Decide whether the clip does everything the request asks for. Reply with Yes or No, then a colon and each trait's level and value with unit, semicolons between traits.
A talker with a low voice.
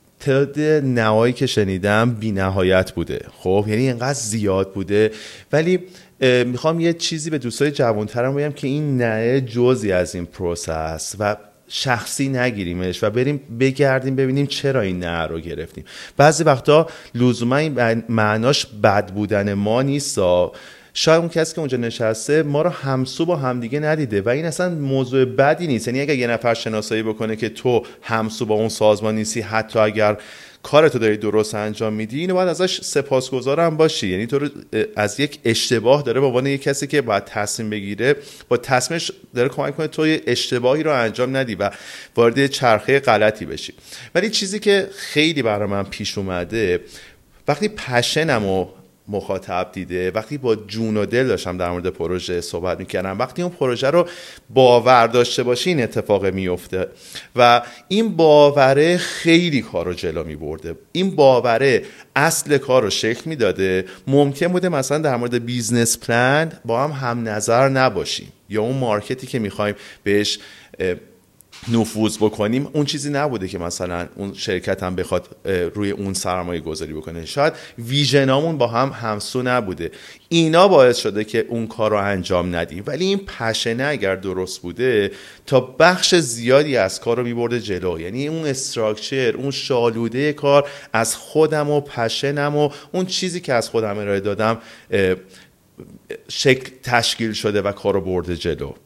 Yes: low, 120 Hz